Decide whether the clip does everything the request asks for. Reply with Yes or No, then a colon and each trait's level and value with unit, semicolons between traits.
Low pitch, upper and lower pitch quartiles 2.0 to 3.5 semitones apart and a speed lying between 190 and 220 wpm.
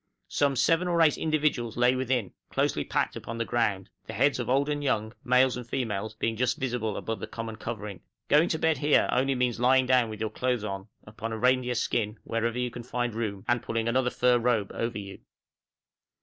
Yes: low, 120 Hz; narrow, 2.6 semitones; fast, 205 wpm